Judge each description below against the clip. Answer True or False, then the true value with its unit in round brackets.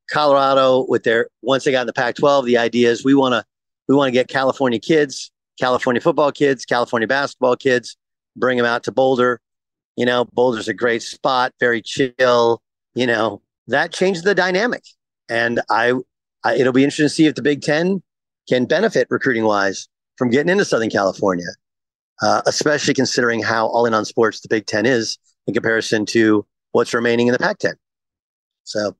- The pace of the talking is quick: False (185 wpm)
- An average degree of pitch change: True (3.0 semitones)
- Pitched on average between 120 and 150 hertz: True (125 Hz)